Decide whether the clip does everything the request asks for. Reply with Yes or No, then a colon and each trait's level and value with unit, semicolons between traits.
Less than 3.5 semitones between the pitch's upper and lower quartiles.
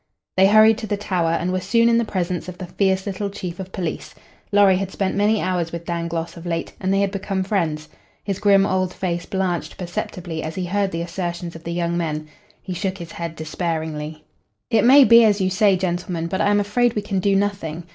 Yes: average, 2.9 semitones